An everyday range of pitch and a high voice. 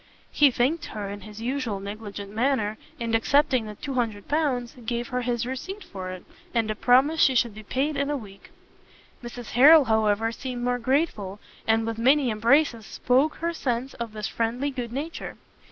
Yes: average, 3.8 semitones; high, 240 Hz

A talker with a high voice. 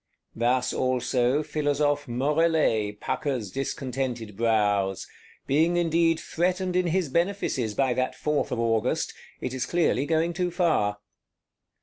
No: low, 135 Hz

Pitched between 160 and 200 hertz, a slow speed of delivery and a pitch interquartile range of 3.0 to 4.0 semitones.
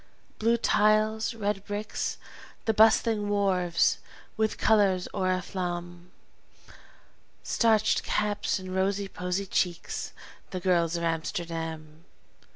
Yes: high, 190 Hz; slow, 95 wpm; average, 3.3 semitones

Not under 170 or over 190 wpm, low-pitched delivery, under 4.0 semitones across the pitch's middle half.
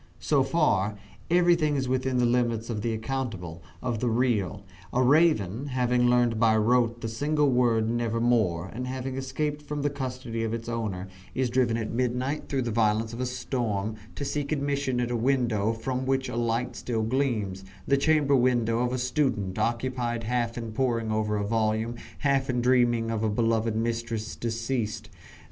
Yes: average, 175 wpm; low, 120 Hz; average, 2.7 semitones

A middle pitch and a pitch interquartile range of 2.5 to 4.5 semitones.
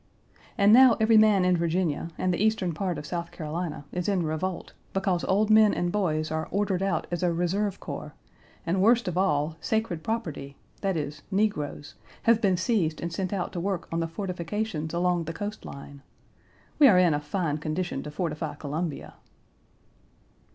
Yes: medium, 180 Hz; average, 4.1 semitones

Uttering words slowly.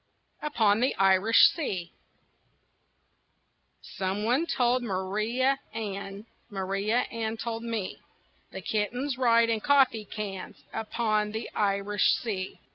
Yes: slow, 110 wpm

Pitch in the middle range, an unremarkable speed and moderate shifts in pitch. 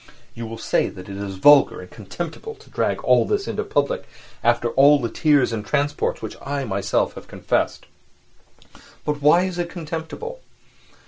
No: medium, 145 Hz; average, 170 wpm; wide, 6.9 semitones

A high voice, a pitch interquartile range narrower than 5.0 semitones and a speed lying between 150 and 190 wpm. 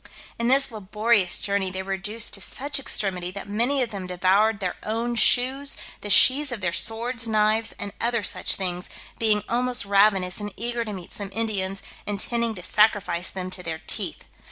Yes: high, 210 Hz; average, 3.4 semitones; average, 180 wpm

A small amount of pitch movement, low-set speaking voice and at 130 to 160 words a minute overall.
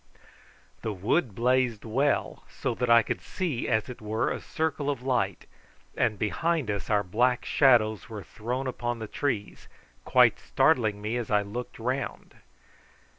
No: average, 3.3 semitones; low, 120 Hz; average, 155 wpm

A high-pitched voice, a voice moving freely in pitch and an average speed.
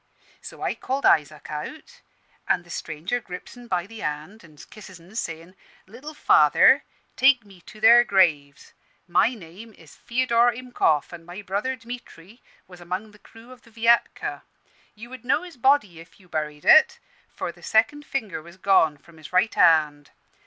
Yes: high, 200 Hz; wide, 6.3 semitones; average, 175 wpm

